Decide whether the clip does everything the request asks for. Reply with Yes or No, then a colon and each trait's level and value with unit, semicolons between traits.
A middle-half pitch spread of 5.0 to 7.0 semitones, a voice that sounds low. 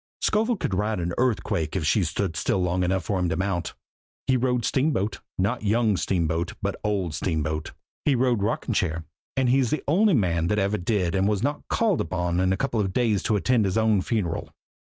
Yes: average, 5.3 semitones; low, 100 Hz